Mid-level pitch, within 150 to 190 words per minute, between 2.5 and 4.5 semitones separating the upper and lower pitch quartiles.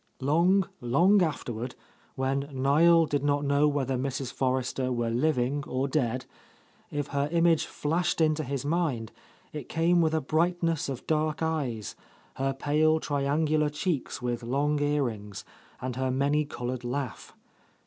No: medium, 145 Hz; average, 140 wpm; average, 3.5 semitones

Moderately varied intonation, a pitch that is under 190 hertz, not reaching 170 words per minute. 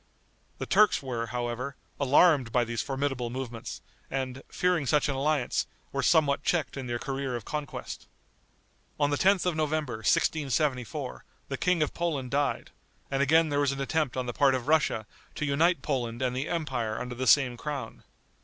No: average, 3.3 semitones; low, 135 Hz; average, 175 wpm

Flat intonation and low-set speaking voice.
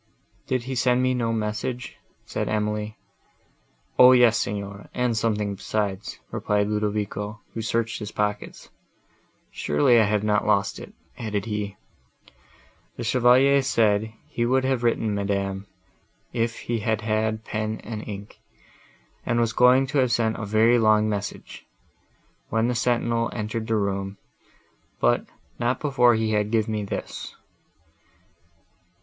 Yes: narrow, 2.3 semitones; low, 110 Hz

